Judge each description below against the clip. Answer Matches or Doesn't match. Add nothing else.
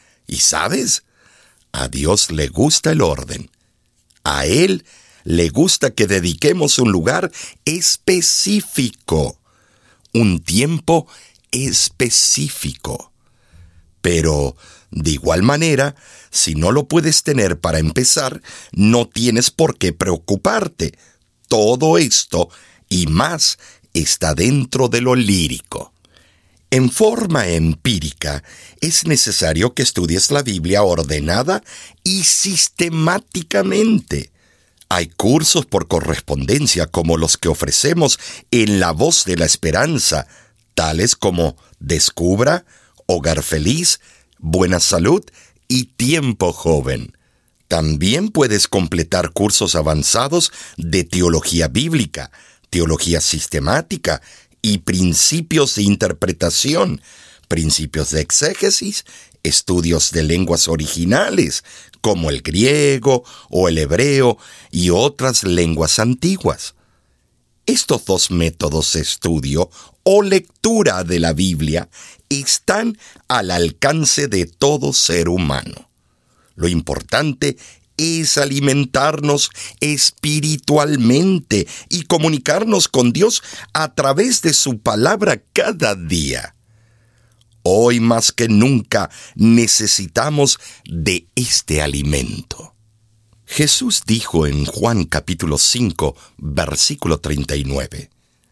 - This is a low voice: Matches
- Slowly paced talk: Matches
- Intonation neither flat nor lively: Doesn't match